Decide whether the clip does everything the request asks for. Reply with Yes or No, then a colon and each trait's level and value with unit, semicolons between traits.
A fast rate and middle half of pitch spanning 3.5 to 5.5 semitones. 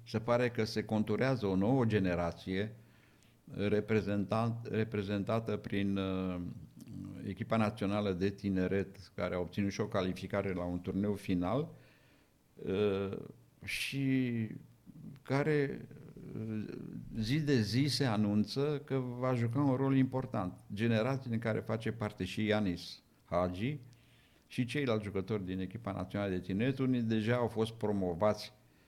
No: average, 125 wpm; average, 3.8 semitones